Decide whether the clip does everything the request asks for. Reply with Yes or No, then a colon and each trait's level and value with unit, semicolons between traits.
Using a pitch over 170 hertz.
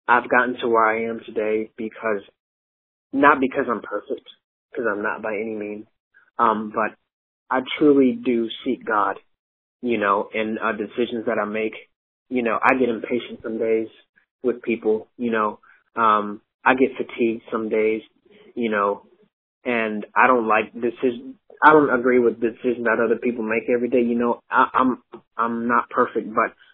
No: low, 115 Hz